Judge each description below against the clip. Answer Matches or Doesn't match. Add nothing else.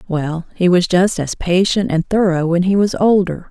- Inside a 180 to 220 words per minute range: Matches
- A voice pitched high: Doesn't match